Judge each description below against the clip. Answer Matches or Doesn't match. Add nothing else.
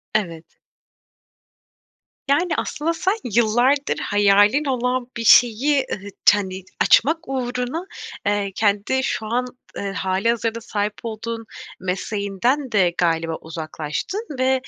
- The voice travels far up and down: Doesn't match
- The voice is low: Doesn't match